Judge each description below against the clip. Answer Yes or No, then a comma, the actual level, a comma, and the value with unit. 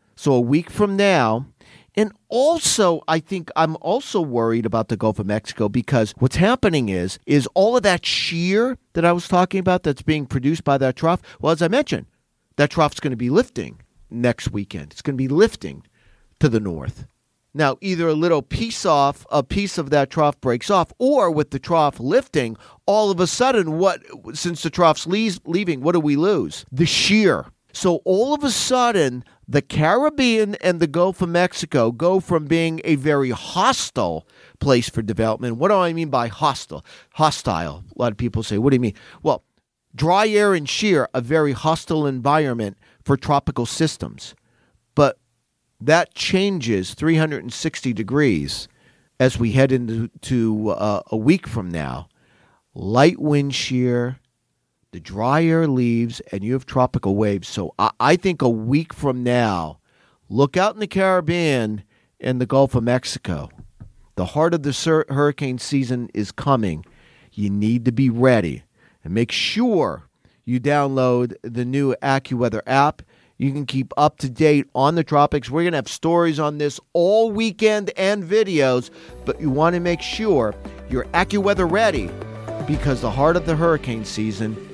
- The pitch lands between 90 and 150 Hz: Yes, medium, 140 Hz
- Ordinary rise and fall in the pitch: No, wide, 6.3 semitones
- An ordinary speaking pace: Yes, average, 170 wpm